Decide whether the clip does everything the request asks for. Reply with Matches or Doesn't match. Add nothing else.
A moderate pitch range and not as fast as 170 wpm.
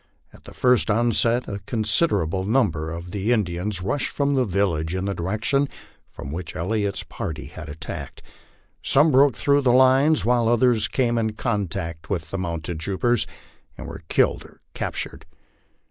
Doesn't match